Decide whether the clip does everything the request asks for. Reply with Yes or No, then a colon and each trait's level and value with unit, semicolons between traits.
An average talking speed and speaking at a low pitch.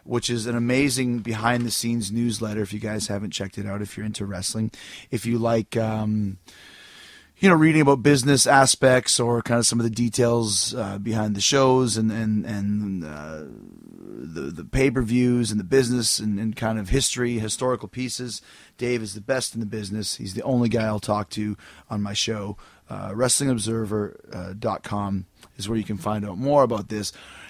Yes: average, 190 wpm; low, 110 Hz